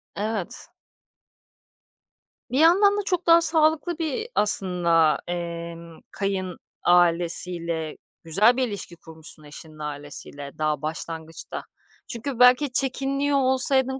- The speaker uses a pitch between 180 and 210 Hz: Yes, high, 190 Hz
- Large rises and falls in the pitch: Yes, wide, 8.5 semitones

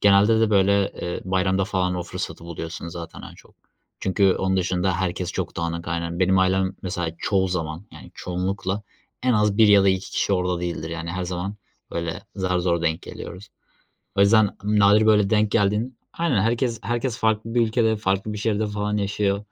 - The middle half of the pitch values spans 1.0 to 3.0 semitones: Yes, average, 2.7 semitones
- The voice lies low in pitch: Yes, very low, 95 Hz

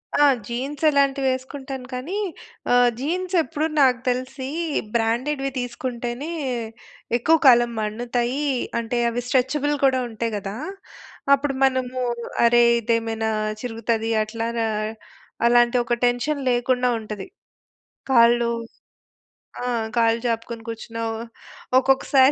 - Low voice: No, high, 245 Hz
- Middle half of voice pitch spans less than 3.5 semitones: Yes, narrow, 2.4 semitones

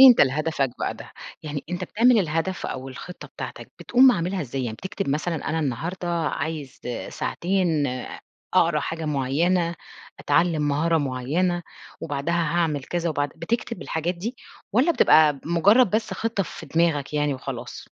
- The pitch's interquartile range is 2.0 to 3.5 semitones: No, average, 3.9 semitones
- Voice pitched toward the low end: No, medium, 165 Hz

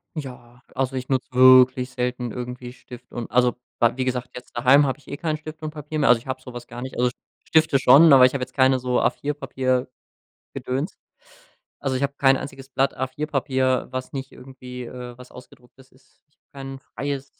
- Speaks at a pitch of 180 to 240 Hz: No, low, 130 Hz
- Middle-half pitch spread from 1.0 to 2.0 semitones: Yes, narrow, 1.5 semitones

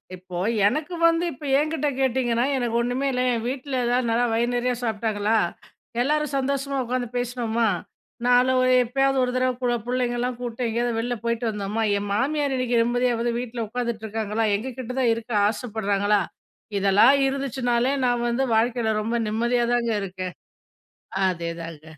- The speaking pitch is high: Yes, high, 240 Hz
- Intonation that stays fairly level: Yes, narrow, 2.2 semitones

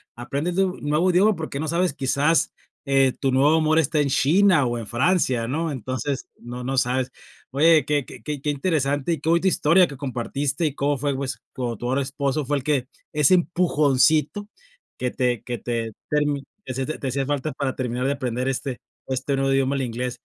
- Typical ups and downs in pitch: Yes, average, 3.1 semitones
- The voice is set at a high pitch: No, medium, 140 Hz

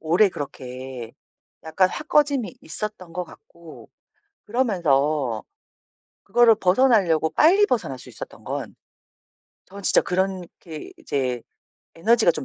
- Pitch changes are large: Yes, wide, 6.6 semitones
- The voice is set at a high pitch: No, medium, 180 Hz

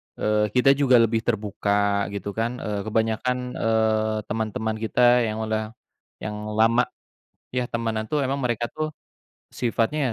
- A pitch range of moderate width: No, narrow, 2.2 semitones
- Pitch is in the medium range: No, low, 110 Hz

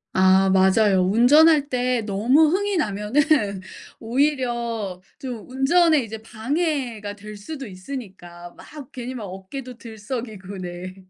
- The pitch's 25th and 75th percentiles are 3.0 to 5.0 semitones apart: No, wide, 5.6 semitones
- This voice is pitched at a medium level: No, high, 230 Hz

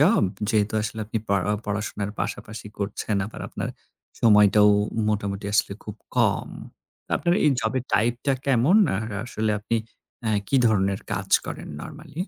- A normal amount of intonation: No, narrow, 2.0 semitones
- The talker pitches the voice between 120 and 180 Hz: No, low, 105 Hz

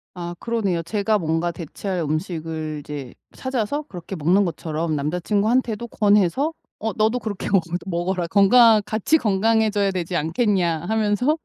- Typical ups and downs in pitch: Yes, average, 4.6 semitones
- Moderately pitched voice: No, high, 195 Hz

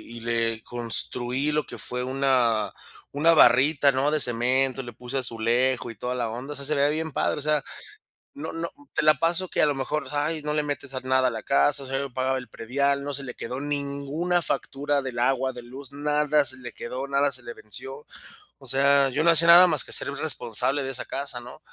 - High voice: No, low, 135 Hz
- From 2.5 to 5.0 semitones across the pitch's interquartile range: Yes, average, 2.8 semitones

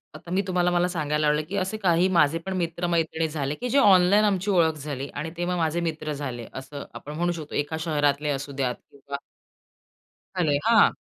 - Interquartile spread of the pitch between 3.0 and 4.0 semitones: Yes, average, 3.5 semitones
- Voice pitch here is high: No, medium, 160 Hz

